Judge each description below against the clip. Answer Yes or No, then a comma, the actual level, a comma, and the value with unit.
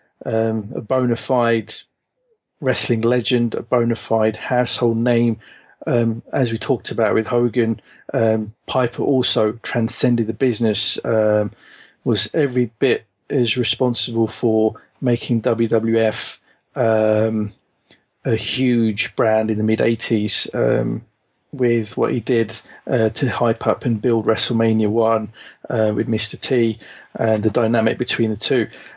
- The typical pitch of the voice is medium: No, low, 115 Hz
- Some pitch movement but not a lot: No, narrow, 1.7 semitones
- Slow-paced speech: Yes, slow, 130 wpm